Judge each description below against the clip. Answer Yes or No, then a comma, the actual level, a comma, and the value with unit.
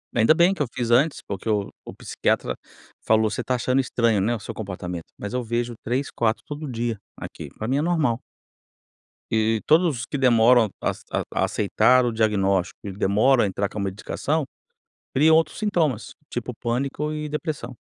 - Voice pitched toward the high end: No, low, 120 Hz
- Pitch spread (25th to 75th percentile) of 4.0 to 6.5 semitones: Yes, average, 4.4 semitones